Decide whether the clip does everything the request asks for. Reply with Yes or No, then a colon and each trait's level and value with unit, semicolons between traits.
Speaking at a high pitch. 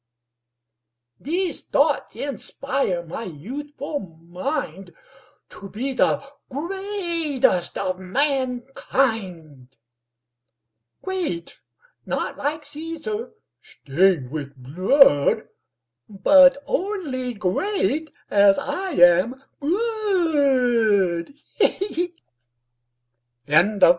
Yes: very high, 260 Hz